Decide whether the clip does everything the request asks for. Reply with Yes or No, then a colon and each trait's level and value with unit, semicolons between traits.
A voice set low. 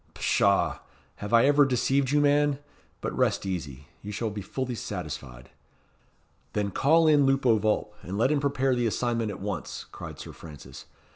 Yes: low, 115 Hz